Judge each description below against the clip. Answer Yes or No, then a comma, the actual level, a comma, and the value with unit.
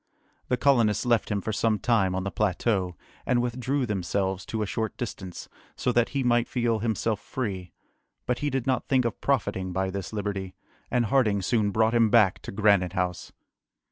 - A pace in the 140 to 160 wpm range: No, average, 185 wpm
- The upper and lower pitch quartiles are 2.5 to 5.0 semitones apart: Yes, average, 3.9 semitones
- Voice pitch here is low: Yes, low, 110 Hz